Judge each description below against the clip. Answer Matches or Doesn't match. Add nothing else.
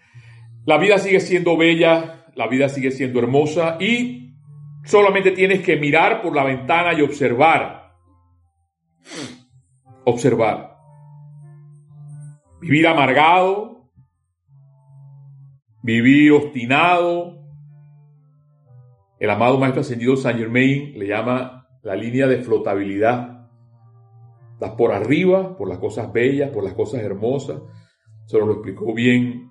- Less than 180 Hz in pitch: Matches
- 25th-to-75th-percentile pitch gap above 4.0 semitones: Doesn't match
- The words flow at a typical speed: Doesn't match